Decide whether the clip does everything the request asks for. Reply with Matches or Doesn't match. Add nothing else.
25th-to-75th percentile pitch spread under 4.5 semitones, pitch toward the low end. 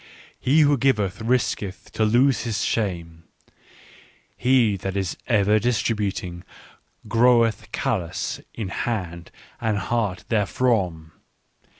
Matches